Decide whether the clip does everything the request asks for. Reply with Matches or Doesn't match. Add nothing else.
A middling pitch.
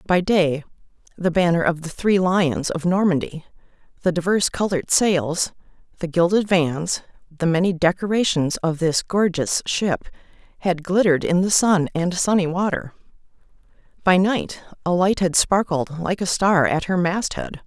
Matches